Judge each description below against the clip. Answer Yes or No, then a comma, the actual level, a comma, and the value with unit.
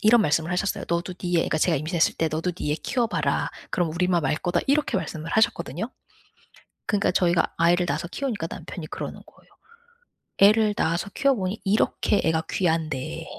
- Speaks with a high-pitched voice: No, medium, 175 Hz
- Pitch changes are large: No, average, 3.8 semitones